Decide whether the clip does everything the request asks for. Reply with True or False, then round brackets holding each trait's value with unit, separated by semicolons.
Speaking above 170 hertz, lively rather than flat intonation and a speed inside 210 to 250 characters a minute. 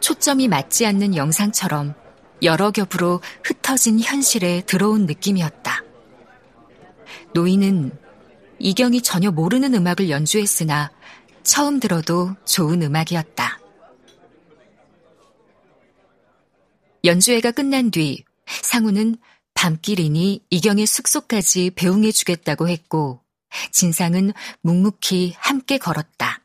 False (190 Hz; 4.6 semitones; 230 characters per minute)